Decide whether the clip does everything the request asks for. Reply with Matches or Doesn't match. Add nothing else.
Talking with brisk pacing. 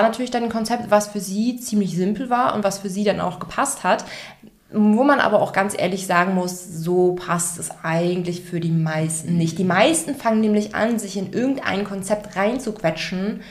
Matches